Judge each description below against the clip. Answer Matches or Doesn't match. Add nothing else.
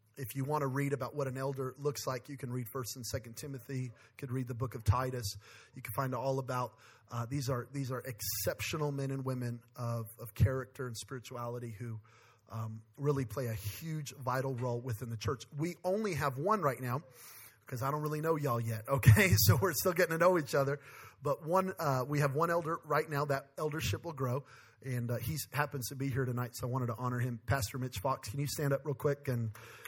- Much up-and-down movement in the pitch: Doesn't match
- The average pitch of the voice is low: Matches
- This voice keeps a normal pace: Doesn't match